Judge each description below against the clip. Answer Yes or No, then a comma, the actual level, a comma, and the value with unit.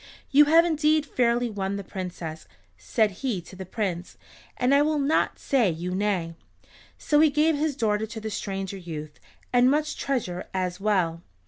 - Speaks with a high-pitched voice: Yes, high, 215 Hz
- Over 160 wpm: Yes, average, 175 wpm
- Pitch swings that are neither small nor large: No, wide, 7.4 semitones